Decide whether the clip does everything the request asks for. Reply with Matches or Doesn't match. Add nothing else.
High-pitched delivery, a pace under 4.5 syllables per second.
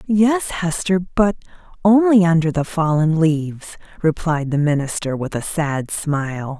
Doesn't match